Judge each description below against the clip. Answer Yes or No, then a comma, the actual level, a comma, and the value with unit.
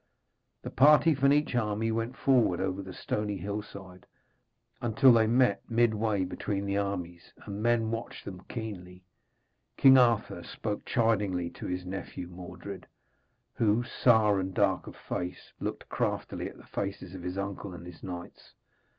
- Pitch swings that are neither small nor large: Yes, average, 3.7 semitones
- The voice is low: Yes, low, 100 Hz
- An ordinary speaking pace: Yes, average, 150 wpm